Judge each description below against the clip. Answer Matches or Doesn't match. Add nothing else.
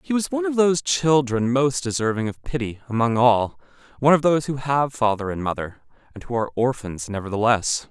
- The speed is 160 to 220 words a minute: Matches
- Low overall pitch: Matches